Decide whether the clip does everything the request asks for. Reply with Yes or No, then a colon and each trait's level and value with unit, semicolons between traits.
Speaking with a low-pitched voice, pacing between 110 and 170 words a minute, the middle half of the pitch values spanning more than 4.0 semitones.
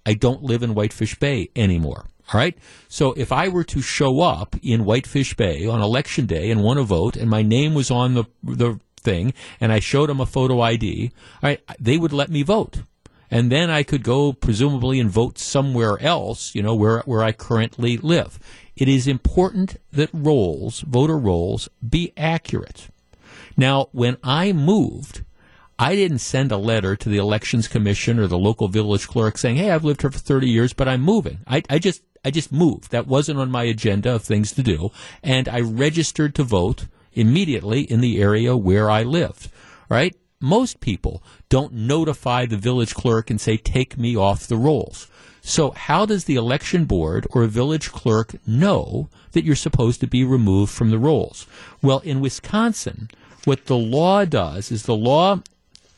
No: low, 125 Hz; average, 190 wpm; average, 4.6 semitones